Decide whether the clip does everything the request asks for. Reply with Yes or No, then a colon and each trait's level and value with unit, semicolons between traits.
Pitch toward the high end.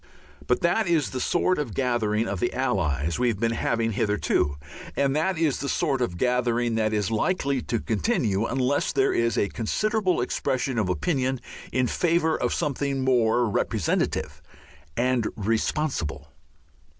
No: low, 125 Hz